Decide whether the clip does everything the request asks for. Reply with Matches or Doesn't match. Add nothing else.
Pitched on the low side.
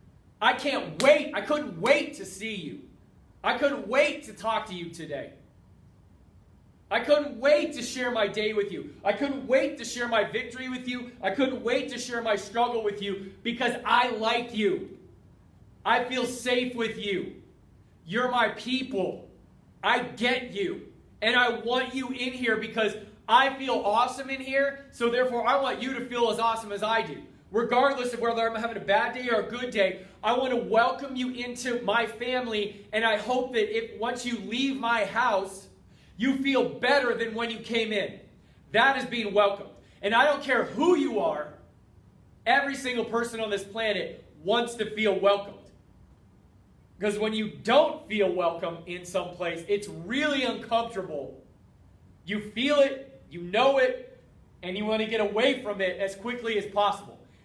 Doesn't match